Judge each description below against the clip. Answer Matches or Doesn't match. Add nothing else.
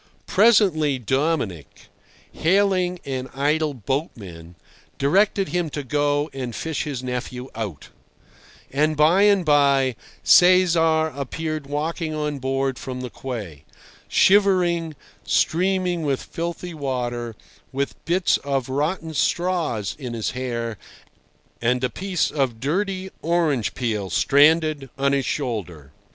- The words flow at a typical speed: Doesn't match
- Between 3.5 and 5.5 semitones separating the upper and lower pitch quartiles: Matches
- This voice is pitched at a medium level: Matches